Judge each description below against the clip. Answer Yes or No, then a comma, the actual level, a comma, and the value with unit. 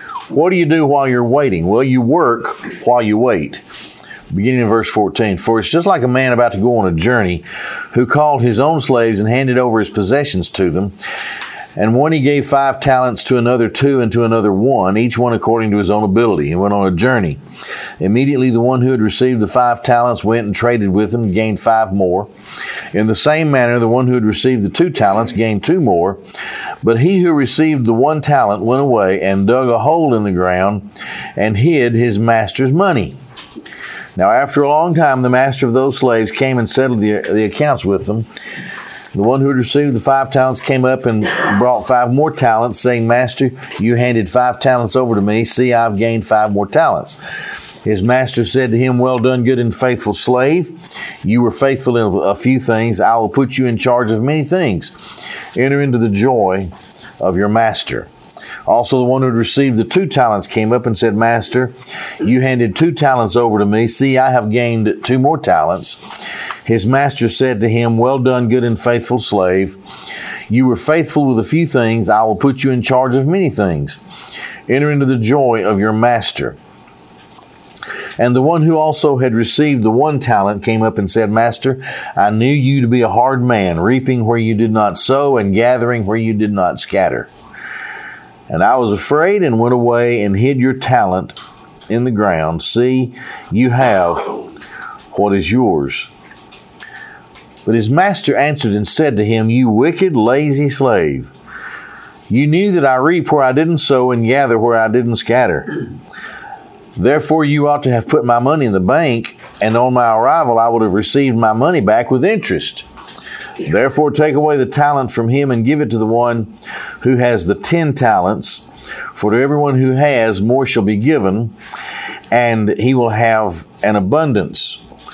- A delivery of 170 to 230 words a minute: Yes, average, 195 wpm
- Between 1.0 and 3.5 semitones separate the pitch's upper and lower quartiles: Yes, average, 3.2 semitones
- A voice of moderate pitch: No, low, 120 Hz